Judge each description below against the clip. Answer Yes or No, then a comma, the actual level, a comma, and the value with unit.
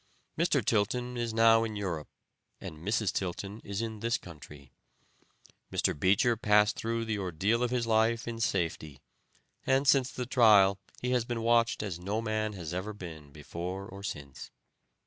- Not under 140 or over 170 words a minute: Yes, average, 165 wpm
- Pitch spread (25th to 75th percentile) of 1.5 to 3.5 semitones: No, average, 4.1 semitones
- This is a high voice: No, low, 105 Hz